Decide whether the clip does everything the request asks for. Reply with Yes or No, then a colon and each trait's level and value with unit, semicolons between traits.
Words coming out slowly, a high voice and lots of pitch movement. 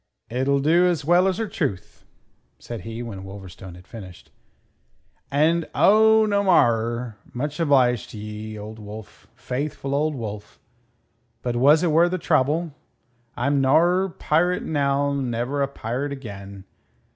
No: slow, 125 wpm; medium, 140 Hz; wide, 6.3 semitones